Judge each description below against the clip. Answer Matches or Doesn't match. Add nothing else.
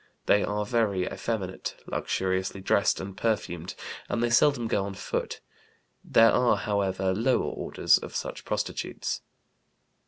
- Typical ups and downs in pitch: Matches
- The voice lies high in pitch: Doesn't match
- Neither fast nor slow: Doesn't match